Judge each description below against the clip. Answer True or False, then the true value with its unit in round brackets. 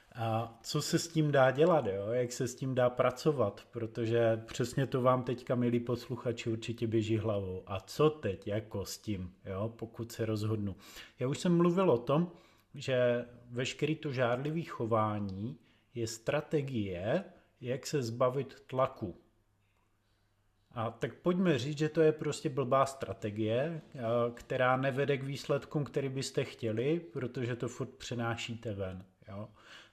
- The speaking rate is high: False (150 wpm)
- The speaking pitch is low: True (120 Hz)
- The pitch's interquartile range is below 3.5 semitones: False (3.9 semitones)